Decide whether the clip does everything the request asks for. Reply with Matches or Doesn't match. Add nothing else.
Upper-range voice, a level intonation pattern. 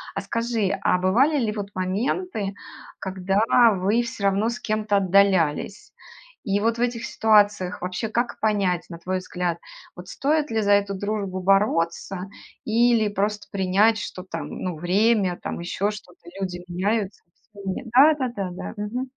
Doesn't match